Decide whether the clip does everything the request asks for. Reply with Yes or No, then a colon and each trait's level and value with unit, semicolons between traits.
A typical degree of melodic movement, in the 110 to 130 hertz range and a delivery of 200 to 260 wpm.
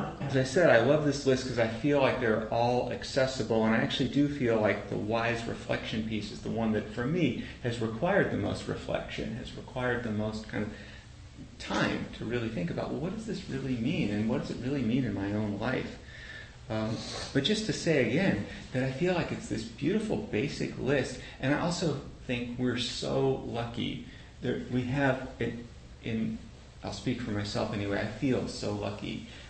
Yes: average, 3.2 semitones; low, 120 Hz; fast, 205 wpm